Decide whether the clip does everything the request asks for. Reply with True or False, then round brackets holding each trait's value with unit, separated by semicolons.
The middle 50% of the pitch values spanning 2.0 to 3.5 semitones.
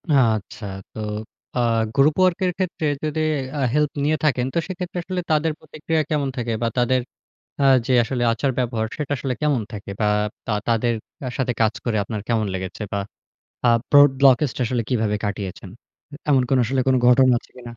False (4.4 semitones)